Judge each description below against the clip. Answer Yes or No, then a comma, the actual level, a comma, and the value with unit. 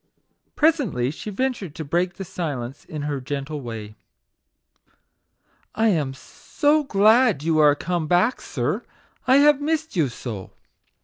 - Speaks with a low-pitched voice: No, medium, 170 Hz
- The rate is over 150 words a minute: No, average, 145 wpm